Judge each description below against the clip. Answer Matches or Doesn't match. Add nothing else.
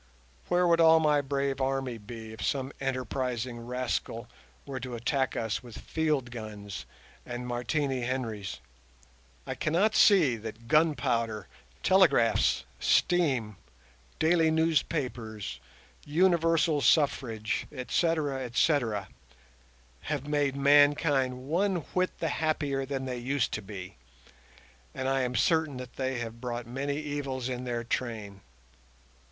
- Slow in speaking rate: Matches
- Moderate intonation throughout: Matches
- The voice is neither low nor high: Doesn't match